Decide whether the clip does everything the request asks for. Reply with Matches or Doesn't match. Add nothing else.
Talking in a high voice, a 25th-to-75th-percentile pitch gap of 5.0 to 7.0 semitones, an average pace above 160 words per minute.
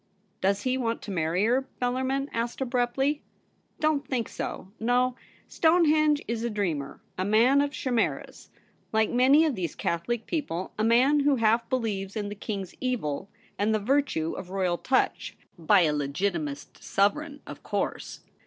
Matches